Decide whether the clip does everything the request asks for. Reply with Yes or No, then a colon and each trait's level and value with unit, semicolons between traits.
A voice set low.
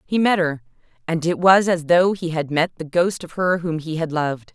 No: medium, 165 Hz